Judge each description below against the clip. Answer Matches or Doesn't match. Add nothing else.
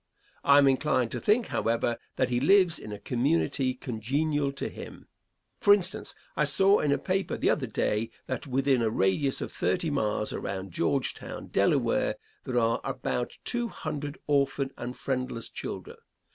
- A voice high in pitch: Doesn't match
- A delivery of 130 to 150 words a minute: Doesn't match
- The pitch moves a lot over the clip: Doesn't match